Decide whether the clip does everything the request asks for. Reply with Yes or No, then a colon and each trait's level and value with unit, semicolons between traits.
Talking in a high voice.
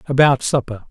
No: low, 130 Hz